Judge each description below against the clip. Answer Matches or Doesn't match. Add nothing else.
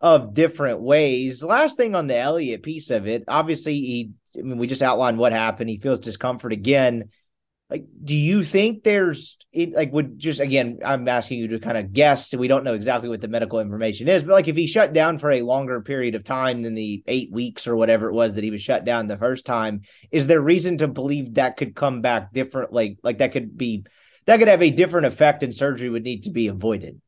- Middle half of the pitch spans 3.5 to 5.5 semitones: Matches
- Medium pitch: Doesn't match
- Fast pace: Matches